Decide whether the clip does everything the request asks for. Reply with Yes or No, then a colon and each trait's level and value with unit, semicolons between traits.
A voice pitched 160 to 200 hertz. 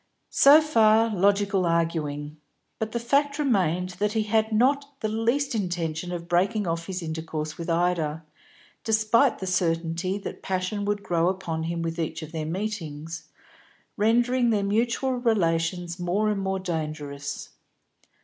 Yes: medium, 185 Hz